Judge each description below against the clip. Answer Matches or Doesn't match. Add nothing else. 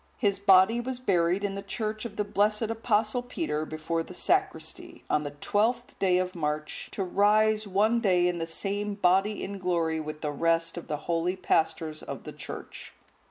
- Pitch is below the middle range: Doesn't match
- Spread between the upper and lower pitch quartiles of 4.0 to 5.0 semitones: Matches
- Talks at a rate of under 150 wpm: Doesn't match